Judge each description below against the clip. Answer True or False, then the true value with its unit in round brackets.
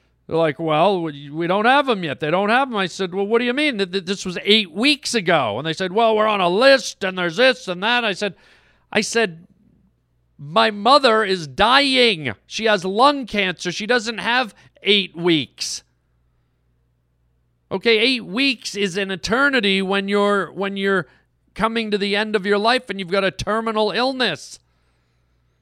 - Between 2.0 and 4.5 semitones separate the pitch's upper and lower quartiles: False (5.3 semitones)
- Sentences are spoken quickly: False (180 wpm)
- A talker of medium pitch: False (200 Hz)